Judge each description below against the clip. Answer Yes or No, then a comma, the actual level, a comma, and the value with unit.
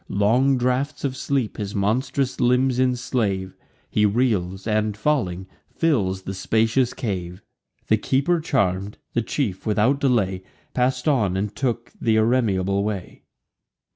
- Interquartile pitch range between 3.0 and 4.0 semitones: No, average, 4.6 semitones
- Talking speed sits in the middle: No, slow, 130 wpm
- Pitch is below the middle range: Yes, low, 110 Hz